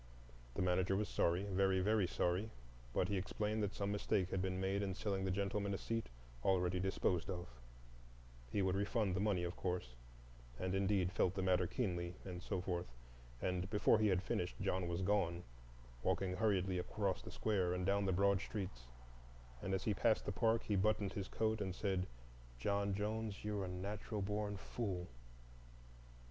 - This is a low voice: Yes, very low, 95 Hz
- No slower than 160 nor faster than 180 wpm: Yes, average, 170 wpm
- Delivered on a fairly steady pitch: Yes, narrow, 2.1 semitones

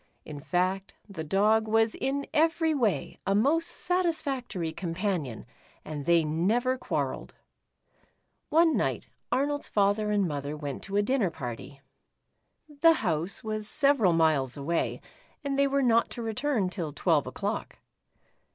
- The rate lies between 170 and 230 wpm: No, slow, 135 wpm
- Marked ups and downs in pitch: Yes, wide, 8.7 semitones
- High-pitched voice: Yes, high, 205 Hz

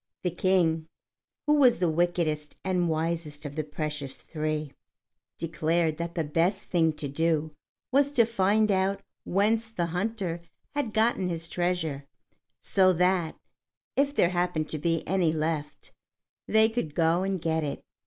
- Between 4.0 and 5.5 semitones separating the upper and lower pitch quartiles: No, average, 3.4 semitones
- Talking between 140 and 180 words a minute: Yes, average, 150 wpm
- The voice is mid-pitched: Yes, medium, 170 Hz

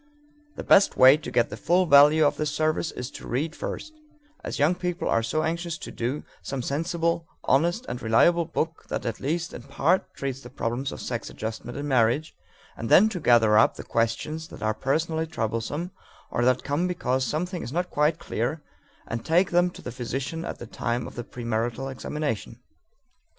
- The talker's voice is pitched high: No, medium, 145 Hz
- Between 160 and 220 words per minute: Yes, average, 190 wpm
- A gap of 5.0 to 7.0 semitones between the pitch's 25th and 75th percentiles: Yes, wide, 5.4 semitones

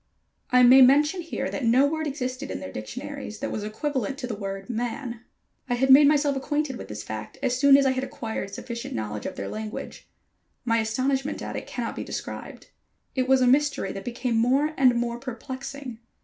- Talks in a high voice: Yes, very high, 255 Hz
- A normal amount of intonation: Yes, average, 3.6 semitones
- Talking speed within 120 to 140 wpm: No, average, 200 wpm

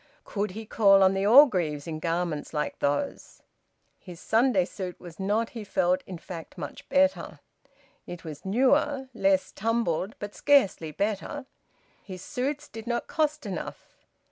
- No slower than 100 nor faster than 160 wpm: Yes, average, 145 wpm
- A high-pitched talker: Yes, high, 195 Hz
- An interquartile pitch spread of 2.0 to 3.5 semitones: No, average, 5.1 semitones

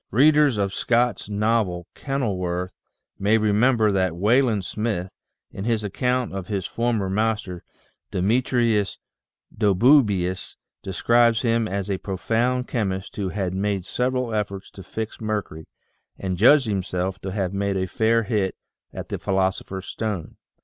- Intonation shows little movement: No, average, 3.4 semitones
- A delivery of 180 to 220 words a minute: No, average, 140 wpm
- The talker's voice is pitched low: Yes, low, 105 Hz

